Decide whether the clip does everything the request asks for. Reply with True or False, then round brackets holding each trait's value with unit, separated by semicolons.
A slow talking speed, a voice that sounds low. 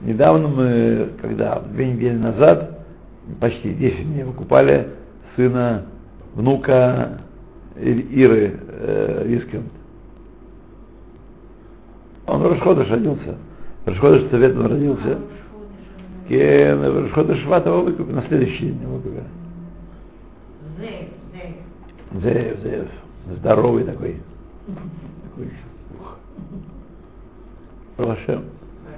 True (65 wpm; 120 Hz)